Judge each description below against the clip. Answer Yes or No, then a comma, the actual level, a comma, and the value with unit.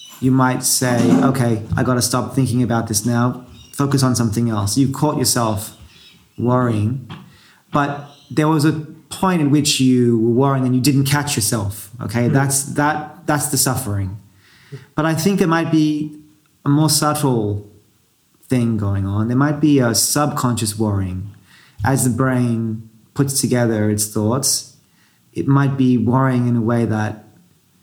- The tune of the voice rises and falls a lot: No, average, 4.0 semitones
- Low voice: Yes, low, 125 Hz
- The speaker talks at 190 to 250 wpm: No, average, 160 wpm